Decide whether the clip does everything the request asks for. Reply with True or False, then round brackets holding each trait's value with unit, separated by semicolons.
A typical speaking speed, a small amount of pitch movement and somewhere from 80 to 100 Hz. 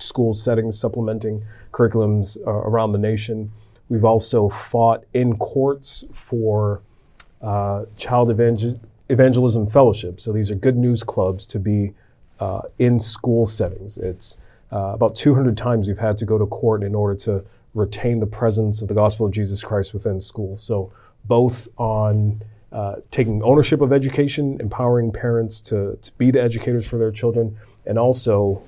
False (160 wpm; 2.3 semitones; 110 Hz)